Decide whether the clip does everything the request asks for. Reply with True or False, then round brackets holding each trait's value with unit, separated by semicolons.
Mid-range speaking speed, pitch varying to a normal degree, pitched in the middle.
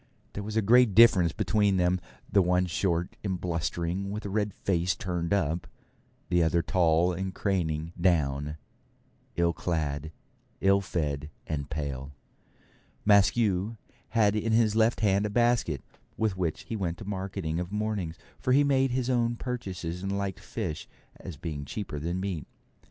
False (155 wpm; 4.0 semitones; 95 Hz)